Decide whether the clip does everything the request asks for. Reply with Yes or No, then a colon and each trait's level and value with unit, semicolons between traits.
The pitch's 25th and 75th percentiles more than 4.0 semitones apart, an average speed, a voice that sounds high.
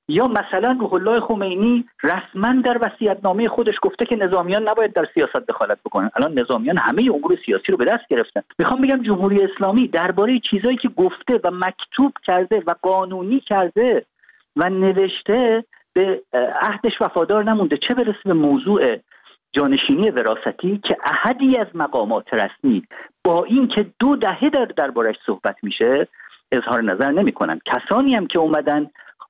Yes: average, 5.1 semitones; average, 145 wpm; high, 220 Hz